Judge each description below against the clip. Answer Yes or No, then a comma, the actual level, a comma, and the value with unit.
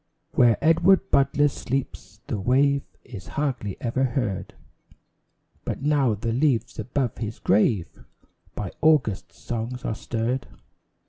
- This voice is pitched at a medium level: No, low, 125 Hz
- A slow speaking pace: Yes, slow, 120 wpm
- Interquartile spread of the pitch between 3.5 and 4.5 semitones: Yes, average, 4.0 semitones